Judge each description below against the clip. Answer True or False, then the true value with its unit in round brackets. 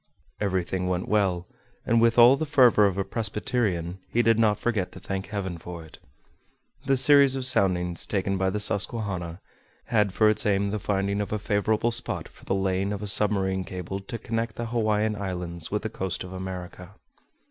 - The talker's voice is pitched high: False (100 Hz)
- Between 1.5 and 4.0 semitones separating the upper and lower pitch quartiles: True (2.9 semitones)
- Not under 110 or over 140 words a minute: False (190 wpm)